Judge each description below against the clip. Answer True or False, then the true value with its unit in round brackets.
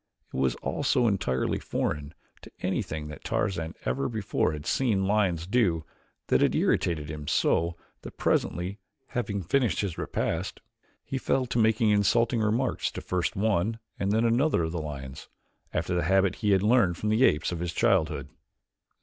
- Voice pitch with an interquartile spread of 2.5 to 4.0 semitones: False (5.5 semitones)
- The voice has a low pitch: True (95 Hz)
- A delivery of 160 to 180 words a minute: True (170 wpm)